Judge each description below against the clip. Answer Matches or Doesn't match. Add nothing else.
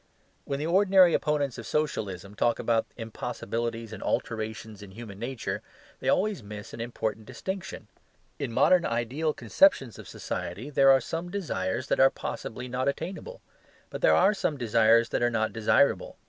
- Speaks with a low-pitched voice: Matches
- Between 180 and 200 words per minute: Doesn't match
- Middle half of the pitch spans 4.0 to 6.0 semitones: Matches